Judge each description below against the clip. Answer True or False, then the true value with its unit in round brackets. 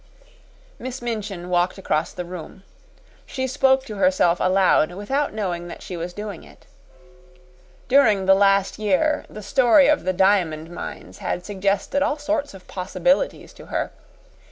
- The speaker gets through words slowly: False (150 wpm)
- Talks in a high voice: True (200 Hz)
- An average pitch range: False (6.4 semitones)